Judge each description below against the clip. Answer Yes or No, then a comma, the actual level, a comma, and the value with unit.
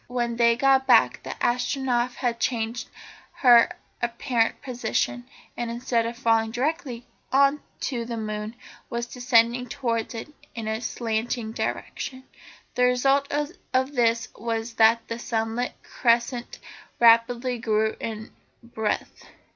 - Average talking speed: No, slow, 125 wpm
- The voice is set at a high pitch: Yes, high, 235 Hz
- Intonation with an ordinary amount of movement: No, narrow, 1.7 semitones